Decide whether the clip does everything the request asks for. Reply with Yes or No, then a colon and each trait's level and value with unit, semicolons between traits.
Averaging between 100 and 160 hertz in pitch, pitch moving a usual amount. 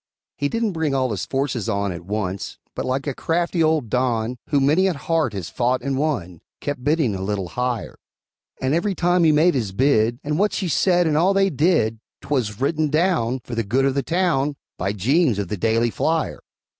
No: low, 135 Hz; wide, 6.2 semitones